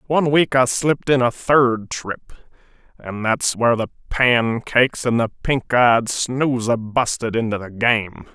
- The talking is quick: No, average, 160 wpm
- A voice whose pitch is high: No, low, 120 Hz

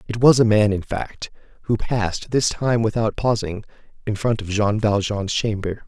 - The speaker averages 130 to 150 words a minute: No, average, 185 wpm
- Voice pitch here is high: No, low, 110 Hz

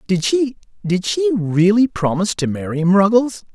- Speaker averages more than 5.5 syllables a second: No, 5.2 syllables/s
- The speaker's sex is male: Yes, male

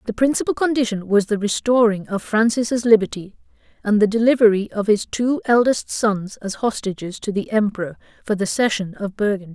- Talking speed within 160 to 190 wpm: Yes, average, 170 wpm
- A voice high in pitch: Yes, high, 215 Hz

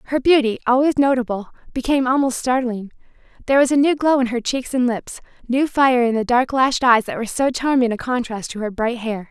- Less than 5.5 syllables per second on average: No, 5.8 syllables/s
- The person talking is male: No, female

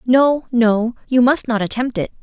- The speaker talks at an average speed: Yes, average, 190 wpm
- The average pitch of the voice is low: No, high, 240 Hz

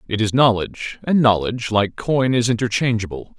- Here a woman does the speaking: No, male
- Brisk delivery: No, average, 160 wpm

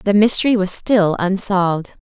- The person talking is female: Yes, female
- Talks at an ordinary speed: Yes, average, 150 wpm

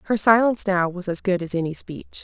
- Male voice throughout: No, female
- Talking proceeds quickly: Yes, fast, 240 wpm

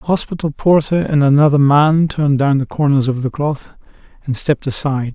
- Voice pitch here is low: No, medium, 145 Hz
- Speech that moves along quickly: No, average, 185 wpm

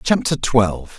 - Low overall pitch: Yes, low, 115 Hz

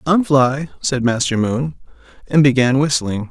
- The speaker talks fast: No, average, 145 wpm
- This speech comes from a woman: No, male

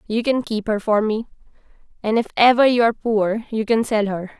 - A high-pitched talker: Yes, high, 220 Hz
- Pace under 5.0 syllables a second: No, 5.3 syllables/s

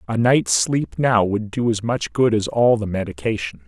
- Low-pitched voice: Yes, low, 110 Hz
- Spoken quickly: Yes, fast, 210 wpm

